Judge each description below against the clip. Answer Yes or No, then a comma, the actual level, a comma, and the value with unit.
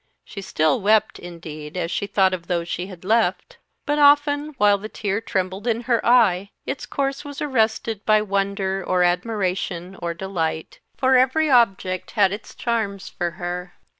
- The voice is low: No, high, 200 Hz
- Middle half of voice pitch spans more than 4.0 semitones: Yes, average, 4.4 semitones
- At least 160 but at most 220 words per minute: Yes, average, 165 wpm